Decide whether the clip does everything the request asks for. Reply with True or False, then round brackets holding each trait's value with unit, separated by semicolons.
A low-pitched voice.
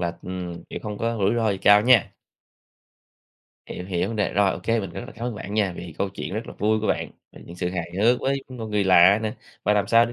True (105 Hz)